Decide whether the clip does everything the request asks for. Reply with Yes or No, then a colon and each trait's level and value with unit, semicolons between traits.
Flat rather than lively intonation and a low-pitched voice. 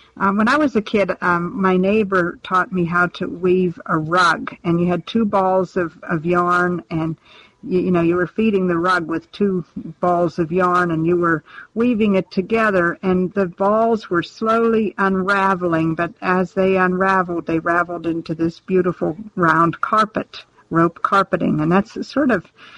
No: narrow, 2.3 semitones; medium, 180 Hz